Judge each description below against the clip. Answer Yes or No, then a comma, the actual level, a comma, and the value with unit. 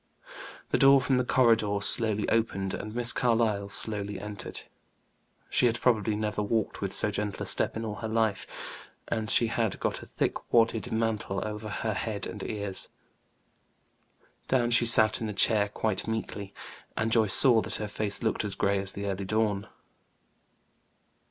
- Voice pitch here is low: Yes, low, 110 Hz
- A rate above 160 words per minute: Yes, average, 170 wpm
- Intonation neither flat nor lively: No, narrow, 1.9 semitones